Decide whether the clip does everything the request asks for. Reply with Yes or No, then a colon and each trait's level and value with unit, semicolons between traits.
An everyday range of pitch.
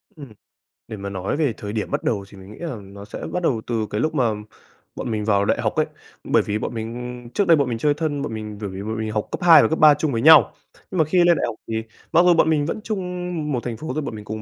No: wide, 6.5 semitones